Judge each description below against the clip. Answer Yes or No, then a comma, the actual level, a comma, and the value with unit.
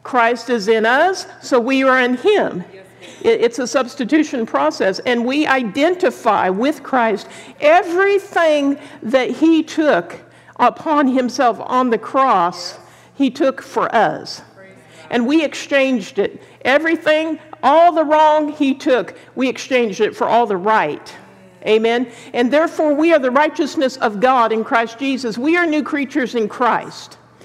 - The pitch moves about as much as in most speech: Yes, average, 4.5 semitones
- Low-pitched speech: No, very high, 270 Hz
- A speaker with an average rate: Yes, average, 145 wpm